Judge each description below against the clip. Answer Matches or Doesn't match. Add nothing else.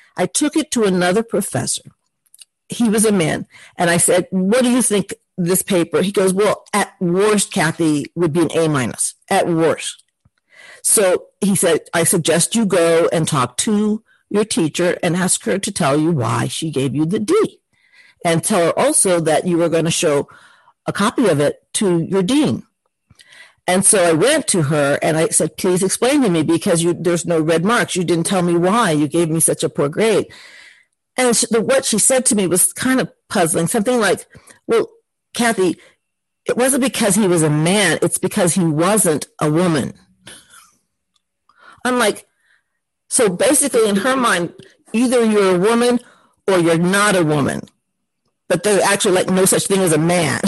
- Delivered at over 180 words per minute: Matches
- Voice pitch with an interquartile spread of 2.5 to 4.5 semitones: Doesn't match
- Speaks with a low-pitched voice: Doesn't match